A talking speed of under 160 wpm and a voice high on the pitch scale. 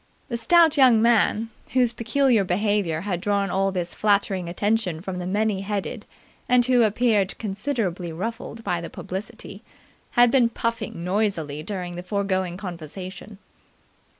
Yes: average, 140 wpm; high, 205 Hz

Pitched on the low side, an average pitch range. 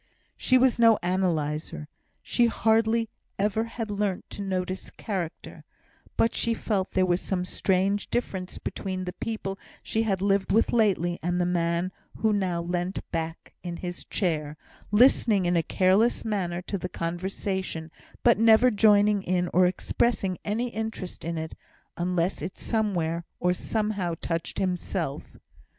No: high, 190 Hz; average, 3.4 semitones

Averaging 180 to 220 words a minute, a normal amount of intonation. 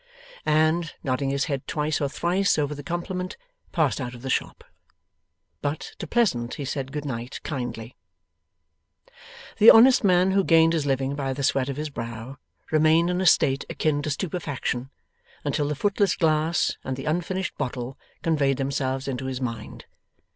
No: average, 165 wpm; average, 3.8 semitones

